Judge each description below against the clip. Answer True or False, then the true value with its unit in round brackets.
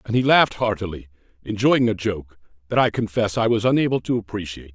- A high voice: False (105 Hz)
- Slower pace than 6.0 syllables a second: False (6.3 syllables/s)